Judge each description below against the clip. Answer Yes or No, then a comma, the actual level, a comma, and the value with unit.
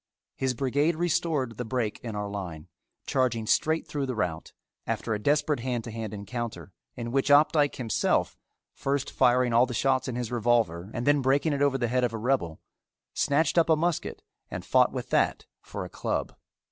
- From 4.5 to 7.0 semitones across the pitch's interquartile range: No, average, 4.0 semitones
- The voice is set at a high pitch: No, low, 125 Hz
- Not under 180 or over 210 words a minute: Yes, average, 190 wpm